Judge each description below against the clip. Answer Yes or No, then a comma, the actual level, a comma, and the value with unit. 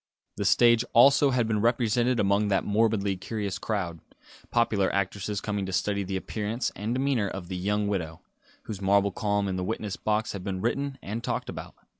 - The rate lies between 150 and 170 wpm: No, average, 185 wpm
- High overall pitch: No, low, 105 Hz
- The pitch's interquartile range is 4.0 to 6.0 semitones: No, average, 2.7 semitones